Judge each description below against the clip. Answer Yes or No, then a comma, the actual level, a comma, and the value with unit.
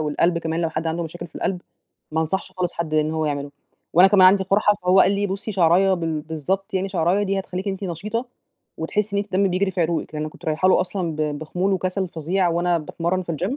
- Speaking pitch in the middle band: Yes, medium, 180 Hz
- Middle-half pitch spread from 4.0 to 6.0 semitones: No, average, 3.1 semitones